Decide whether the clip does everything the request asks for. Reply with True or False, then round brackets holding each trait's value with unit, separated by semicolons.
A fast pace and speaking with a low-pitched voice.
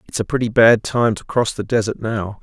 True (245 wpm; 110 Hz)